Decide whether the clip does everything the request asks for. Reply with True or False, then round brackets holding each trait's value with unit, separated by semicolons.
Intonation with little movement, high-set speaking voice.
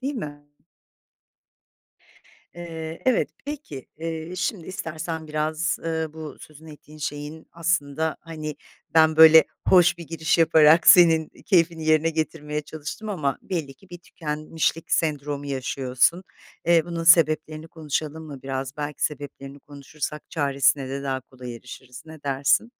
False (2.2 semitones; 155 Hz)